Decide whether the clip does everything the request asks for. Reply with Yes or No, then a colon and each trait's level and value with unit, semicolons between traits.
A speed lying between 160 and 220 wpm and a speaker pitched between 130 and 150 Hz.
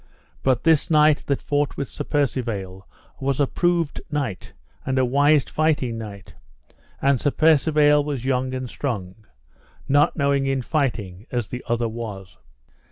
No: average, 150 wpm; low, 135 Hz